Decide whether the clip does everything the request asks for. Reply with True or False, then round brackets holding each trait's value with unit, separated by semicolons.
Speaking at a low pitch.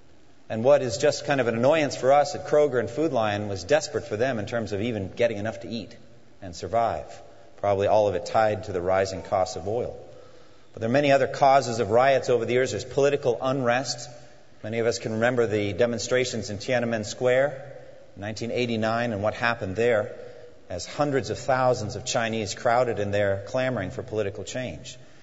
True (115 Hz)